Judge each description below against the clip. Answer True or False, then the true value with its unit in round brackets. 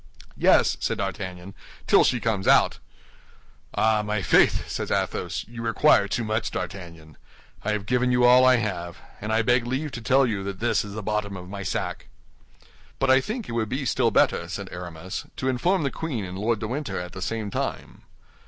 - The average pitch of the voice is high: False (110 Hz)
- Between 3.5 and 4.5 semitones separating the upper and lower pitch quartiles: True (4.2 semitones)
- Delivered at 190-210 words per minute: True (200 wpm)